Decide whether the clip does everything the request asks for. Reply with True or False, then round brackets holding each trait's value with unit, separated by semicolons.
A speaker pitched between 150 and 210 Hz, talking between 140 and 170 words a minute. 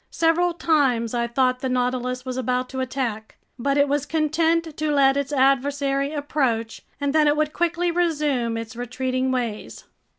False (275 Hz; 165 wpm)